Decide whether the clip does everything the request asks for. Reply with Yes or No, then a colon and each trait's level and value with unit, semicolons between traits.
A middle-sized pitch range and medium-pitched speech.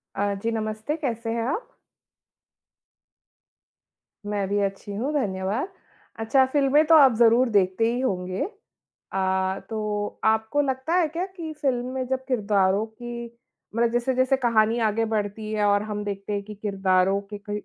No: average, 4.2 semitones; high, 220 Hz